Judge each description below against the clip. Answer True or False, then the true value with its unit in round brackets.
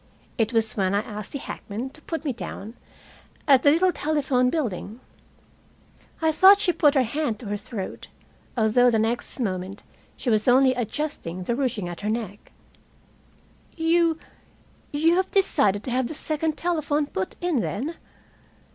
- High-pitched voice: True (250 Hz)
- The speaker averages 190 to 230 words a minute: False (160 wpm)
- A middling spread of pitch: False (6.3 semitones)